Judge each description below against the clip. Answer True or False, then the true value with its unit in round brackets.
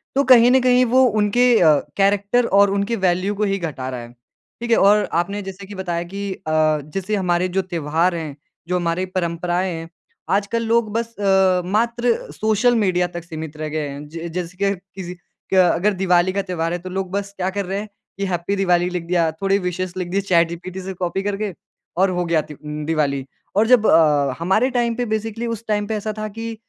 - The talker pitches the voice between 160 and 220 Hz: True (190 Hz)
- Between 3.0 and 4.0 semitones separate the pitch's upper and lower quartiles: True (3.3 semitones)